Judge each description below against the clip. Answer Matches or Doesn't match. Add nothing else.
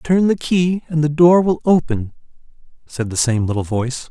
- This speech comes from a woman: Doesn't match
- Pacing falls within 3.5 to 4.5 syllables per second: Doesn't match